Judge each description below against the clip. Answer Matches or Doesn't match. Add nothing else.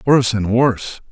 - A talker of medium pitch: Doesn't match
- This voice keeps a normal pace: Matches